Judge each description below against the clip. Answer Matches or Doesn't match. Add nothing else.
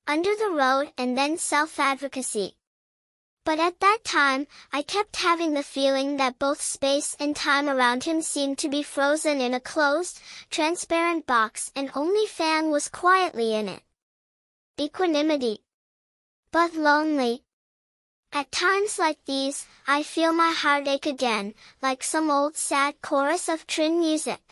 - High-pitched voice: Matches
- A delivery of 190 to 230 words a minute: Doesn't match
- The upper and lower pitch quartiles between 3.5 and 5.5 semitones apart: Doesn't match